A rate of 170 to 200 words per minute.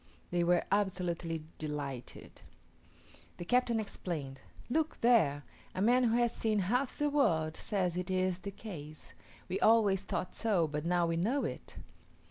No: average, 150 wpm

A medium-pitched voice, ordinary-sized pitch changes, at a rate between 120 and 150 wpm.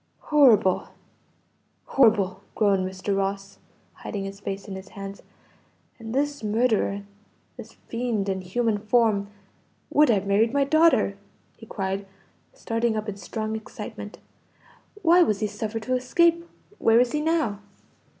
No: high, 215 Hz; average, 4.0 semitones; slow, 135 wpm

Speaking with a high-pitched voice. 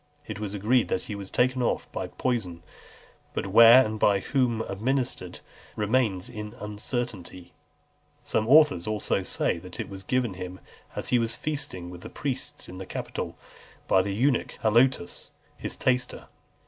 No: low, 110 Hz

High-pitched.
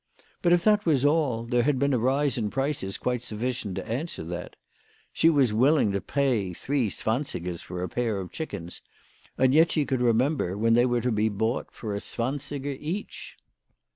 No: low, 125 Hz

